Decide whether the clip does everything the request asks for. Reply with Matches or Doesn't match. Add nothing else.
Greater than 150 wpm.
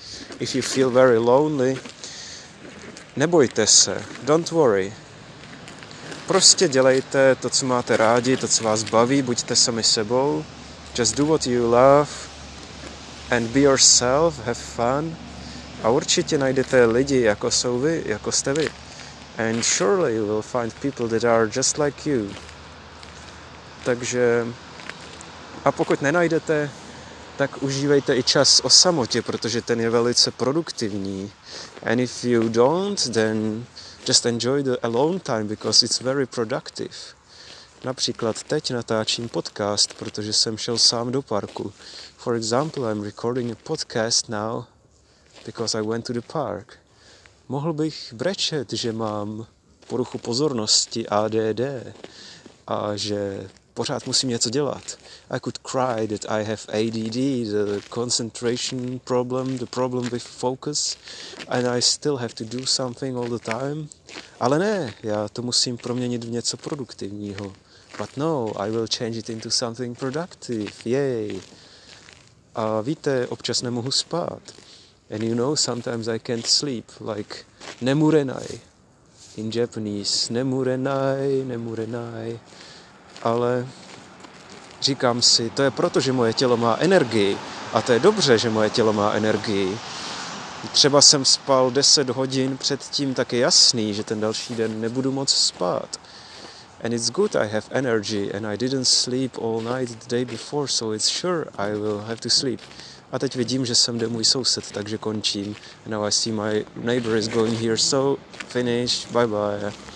Doesn't match